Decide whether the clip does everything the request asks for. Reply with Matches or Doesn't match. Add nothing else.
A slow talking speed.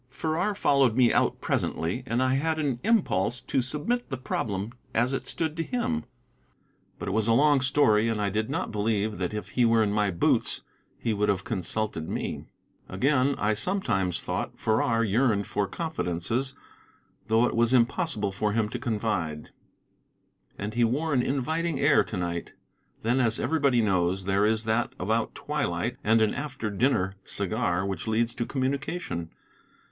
Doesn't match